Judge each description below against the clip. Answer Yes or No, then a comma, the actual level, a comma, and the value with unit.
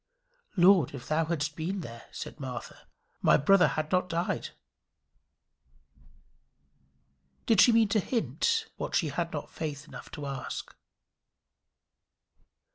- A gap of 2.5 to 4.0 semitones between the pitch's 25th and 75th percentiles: No, average, 4.9 semitones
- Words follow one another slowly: Yes, slow, 120 wpm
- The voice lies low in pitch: No, medium, 165 Hz